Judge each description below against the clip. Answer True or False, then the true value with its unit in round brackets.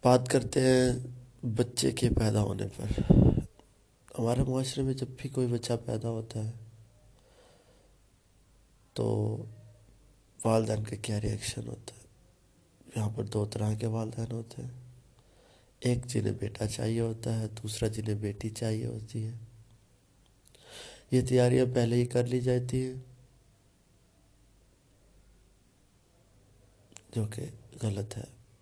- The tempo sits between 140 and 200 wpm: False (120 wpm)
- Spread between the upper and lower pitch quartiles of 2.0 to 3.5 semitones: True (2.5 semitones)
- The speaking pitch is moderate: False (115 Hz)